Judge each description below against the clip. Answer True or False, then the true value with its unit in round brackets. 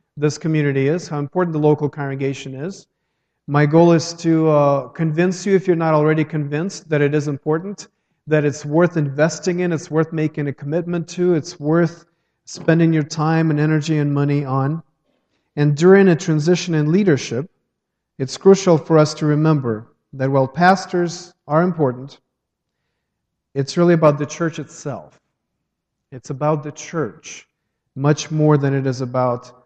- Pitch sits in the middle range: True (155 Hz)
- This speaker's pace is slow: False (160 wpm)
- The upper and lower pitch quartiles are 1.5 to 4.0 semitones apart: True (2.8 semitones)